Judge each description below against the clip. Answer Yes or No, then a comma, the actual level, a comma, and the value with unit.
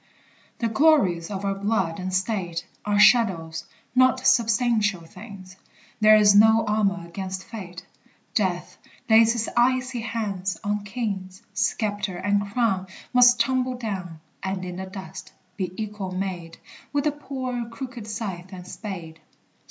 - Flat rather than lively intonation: No, average, 3.7 semitones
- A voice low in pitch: No, high, 205 Hz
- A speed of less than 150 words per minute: Yes, average, 140 wpm